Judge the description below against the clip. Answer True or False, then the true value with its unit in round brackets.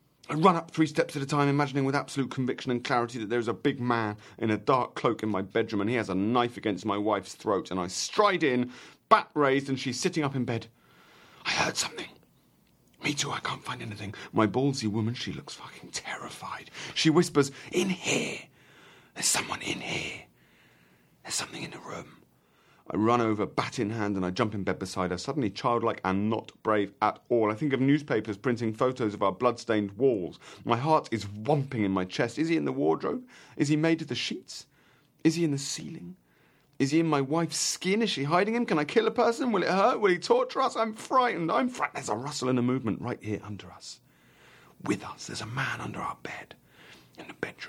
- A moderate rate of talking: False (220 wpm)